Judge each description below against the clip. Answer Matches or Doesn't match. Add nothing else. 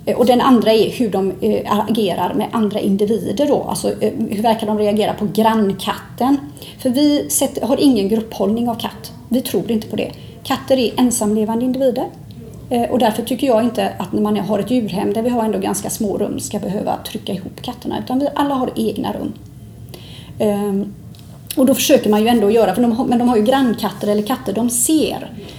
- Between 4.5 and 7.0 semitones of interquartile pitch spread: Doesn't match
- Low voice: Doesn't match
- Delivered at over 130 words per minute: Matches